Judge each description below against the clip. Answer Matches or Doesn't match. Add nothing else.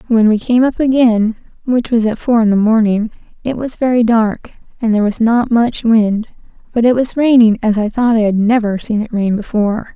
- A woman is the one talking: Matches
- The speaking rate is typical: Doesn't match